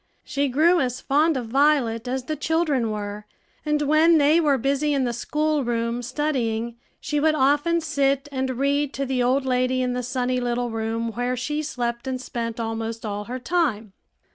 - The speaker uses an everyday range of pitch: Yes, average, 3.7 semitones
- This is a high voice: Yes, very high, 260 Hz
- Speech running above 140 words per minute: Yes, average, 185 wpm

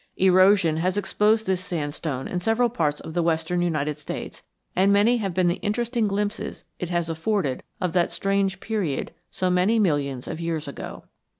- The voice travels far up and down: No, average, 4.1 semitones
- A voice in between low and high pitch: Yes, medium, 180 Hz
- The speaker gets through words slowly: No, average, 175 wpm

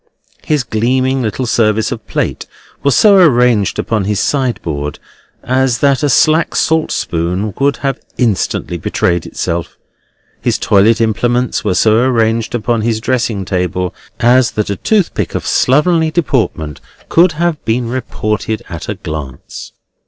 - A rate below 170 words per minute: Yes, average, 140 wpm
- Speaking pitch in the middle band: No, low, 115 Hz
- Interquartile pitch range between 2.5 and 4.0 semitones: No, average, 4.5 semitones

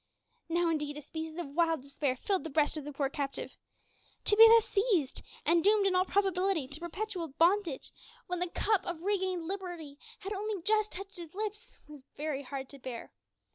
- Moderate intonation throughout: Yes, average, 5.0 semitones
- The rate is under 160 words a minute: No, average, 190 wpm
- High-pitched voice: Yes, very high, 345 Hz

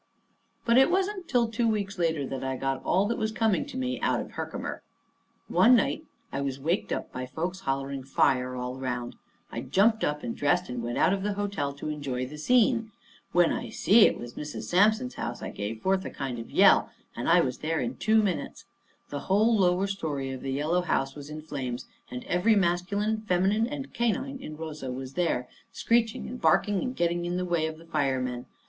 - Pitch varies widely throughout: Yes, wide, 8.1 semitones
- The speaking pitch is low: No, medium, 170 Hz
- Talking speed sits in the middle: No, fast, 210 wpm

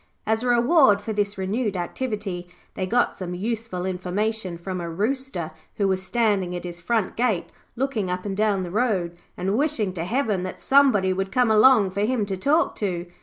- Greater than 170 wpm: Yes, average, 190 wpm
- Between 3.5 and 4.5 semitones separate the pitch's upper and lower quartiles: Yes, average, 4.1 semitones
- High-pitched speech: Yes, high, 205 Hz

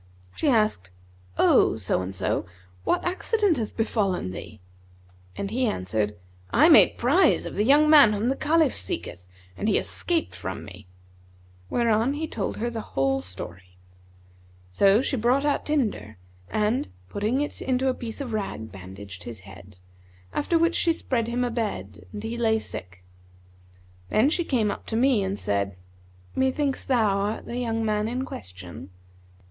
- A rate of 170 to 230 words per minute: No, average, 160 wpm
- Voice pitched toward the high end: Yes, high, 220 Hz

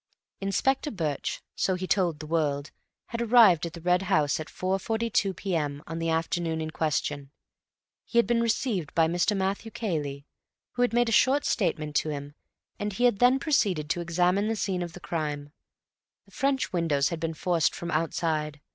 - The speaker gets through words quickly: No, average, 180 wpm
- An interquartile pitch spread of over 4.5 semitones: Yes, average, 5.1 semitones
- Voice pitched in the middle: Yes, medium, 175 Hz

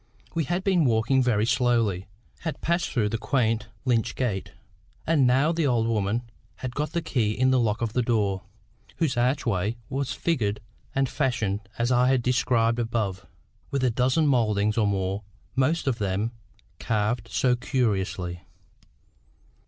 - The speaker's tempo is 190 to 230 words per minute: No, average, 155 wpm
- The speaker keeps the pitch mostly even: No, average, 3.6 semitones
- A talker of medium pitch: No, low, 120 Hz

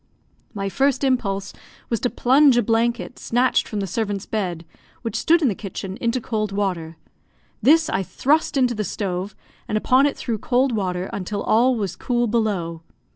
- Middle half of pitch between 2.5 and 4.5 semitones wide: Yes, average, 4.2 semitones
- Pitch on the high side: Yes, high, 220 Hz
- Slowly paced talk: No, average, 175 wpm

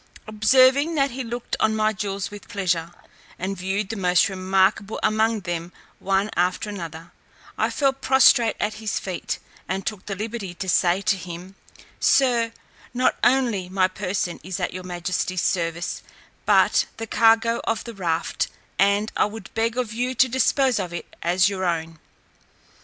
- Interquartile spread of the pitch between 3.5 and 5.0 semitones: Yes, average, 3.8 semitones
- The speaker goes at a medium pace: Yes, average, 165 wpm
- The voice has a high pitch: Yes, high, 200 Hz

